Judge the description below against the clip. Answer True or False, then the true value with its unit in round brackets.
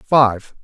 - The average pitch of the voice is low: True (120 Hz)